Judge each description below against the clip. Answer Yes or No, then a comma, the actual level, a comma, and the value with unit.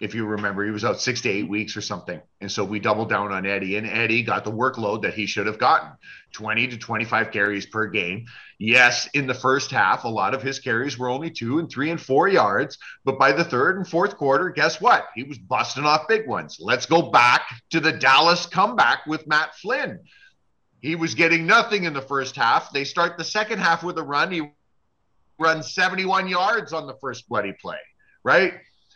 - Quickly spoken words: Yes, fast, 215 wpm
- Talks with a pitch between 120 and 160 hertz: Yes, low, 135 Hz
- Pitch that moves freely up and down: Yes, wide, 7.0 semitones